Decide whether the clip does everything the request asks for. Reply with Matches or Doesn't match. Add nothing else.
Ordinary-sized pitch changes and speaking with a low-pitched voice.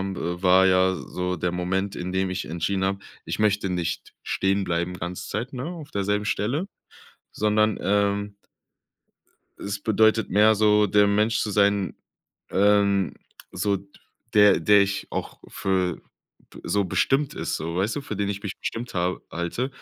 Doesn't match